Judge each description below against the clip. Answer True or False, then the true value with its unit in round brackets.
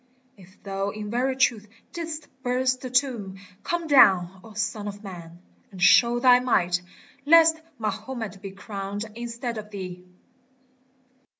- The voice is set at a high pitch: True (215 Hz)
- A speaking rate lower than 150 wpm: True (135 wpm)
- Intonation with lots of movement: False (4.6 semitones)